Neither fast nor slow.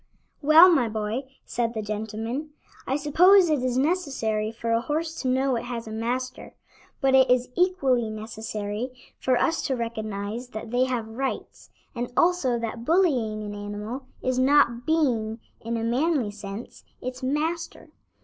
Yes: average, 160 wpm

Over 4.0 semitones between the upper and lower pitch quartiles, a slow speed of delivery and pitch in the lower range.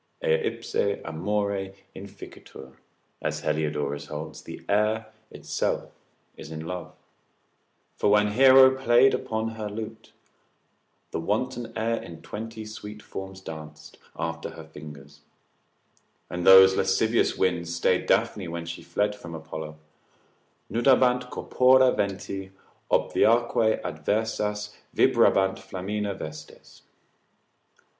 Yes: average, 5.0 semitones; slow, 105 wpm; low, 100 Hz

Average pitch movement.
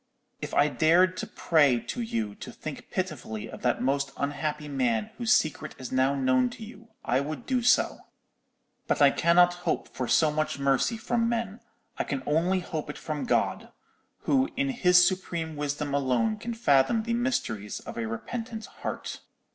No: wide, 8.3 semitones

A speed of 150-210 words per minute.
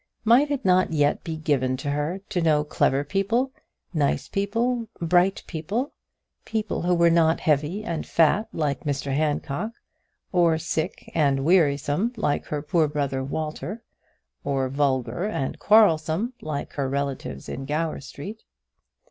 No: average, 140 wpm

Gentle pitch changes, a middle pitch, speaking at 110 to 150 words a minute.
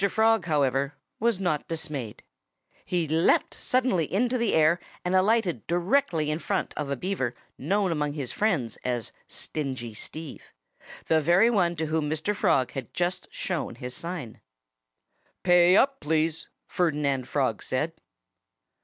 No: average, 4.3 semitones; medium, 160 Hz; average, 140 wpm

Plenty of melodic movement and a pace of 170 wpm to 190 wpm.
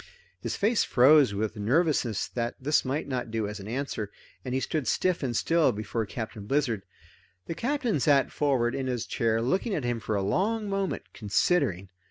Yes: wide, 5.8 semitones; average, 185 wpm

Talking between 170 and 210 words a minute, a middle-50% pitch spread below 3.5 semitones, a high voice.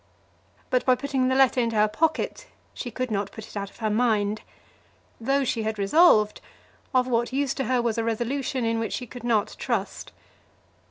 Yes: average, 195 wpm; average, 3.0 semitones; high, 235 Hz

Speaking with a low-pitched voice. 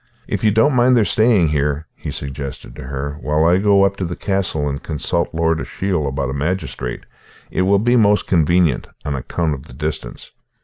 Yes: very low, 80 Hz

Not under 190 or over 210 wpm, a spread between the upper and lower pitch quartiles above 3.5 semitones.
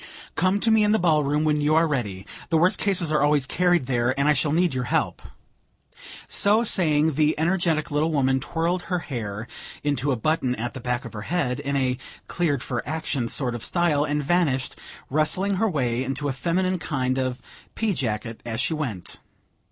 Yes: average, 200 wpm; average, 4.7 semitones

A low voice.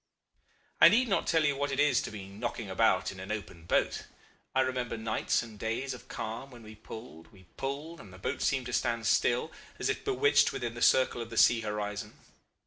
Yes: low, 115 Hz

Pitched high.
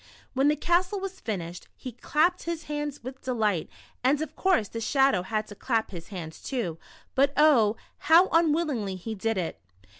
Yes: very high, 260 Hz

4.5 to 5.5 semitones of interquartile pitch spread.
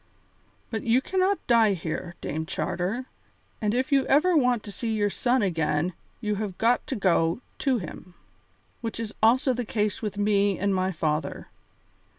Yes: average, 4.9 semitones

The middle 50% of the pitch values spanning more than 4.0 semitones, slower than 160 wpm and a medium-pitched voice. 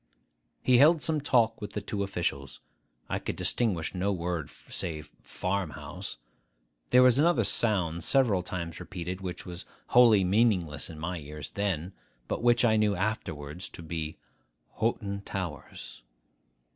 No: average, 4.9 semitones; average, 145 wpm; very low, 95 Hz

